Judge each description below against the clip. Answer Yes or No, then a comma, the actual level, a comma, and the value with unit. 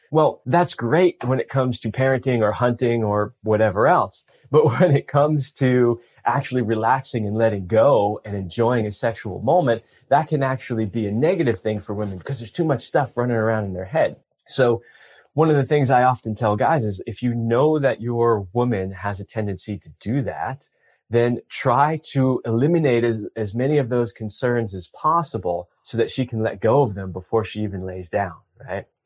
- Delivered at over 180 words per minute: Yes, average, 195 wpm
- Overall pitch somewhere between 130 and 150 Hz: No, low, 120 Hz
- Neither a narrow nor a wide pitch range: Yes, average, 3.8 semitones